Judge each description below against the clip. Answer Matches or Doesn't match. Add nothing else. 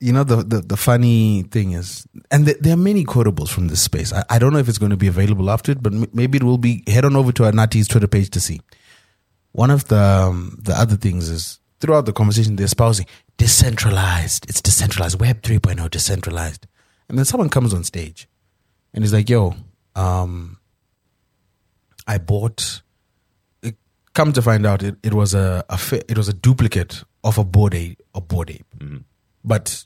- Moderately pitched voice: Doesn't match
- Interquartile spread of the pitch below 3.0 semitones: Doesn't match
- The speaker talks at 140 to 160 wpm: Doesn't match